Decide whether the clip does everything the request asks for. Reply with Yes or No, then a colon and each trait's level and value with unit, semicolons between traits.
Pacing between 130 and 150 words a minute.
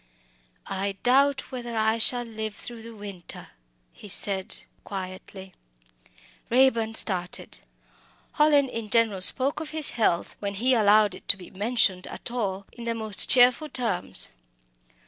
Yes: average, 140 wpm